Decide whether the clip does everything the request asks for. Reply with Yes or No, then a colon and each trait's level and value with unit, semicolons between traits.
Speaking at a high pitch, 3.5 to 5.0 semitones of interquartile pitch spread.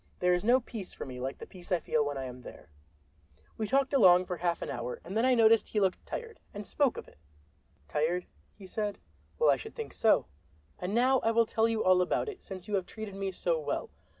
Yes: high, 195 Hz; average, 4.4 semitones